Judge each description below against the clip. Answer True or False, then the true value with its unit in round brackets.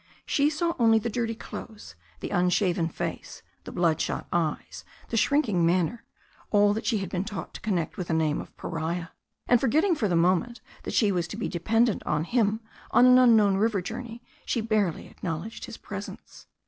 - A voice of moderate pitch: False (205 Hz)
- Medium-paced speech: True (190 wpm)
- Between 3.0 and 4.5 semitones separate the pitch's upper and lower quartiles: False (4.9 semitones)